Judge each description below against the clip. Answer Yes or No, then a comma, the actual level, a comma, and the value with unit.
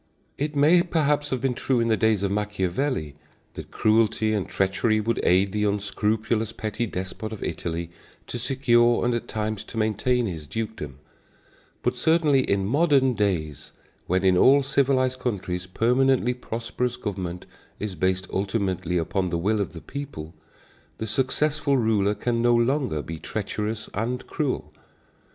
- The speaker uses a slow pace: No, average, 150 wpm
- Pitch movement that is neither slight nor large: Yes, average, 4.8 semitones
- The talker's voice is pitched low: Yes, low, 110 Hz